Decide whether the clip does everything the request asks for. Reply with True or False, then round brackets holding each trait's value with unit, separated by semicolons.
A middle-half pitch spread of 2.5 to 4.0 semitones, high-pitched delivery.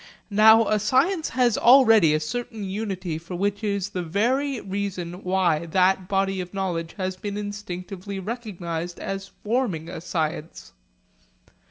True (3.2 semitones; 195 Hz)